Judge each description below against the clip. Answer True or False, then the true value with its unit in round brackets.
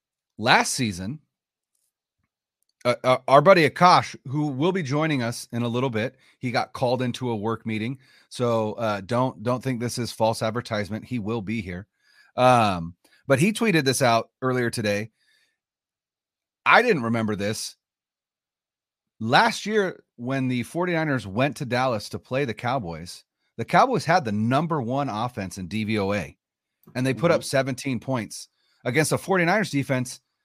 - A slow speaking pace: False (155 wpm)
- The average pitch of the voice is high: False (125 Hz)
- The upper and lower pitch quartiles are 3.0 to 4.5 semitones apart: True (3.6 semitones)